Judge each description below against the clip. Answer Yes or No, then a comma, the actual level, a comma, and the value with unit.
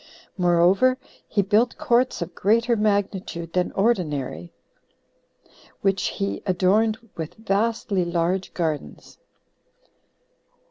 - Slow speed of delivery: Yes, slow, 90 wpm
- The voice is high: Yes, high, 195 Hz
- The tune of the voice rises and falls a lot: No, average, 4.1 semitones